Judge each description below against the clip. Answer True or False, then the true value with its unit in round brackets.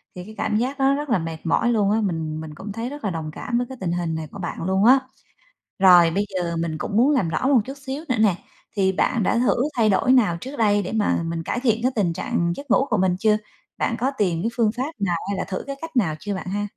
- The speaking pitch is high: True (205 Hz)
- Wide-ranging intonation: True (5.9 semitones)